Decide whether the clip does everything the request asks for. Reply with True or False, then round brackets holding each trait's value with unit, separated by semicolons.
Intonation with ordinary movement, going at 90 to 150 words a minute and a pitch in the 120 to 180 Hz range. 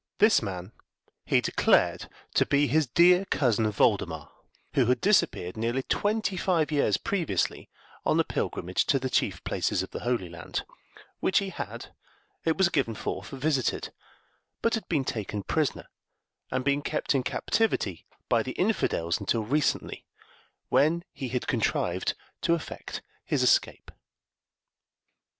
False (6.9 semitones; 140 wpm; 140 Hz)